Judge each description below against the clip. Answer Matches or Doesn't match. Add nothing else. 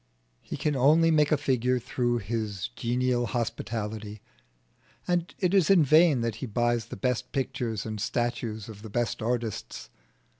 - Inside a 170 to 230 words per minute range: Doesn't match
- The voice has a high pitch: Doesn't match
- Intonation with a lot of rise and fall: Doesn't match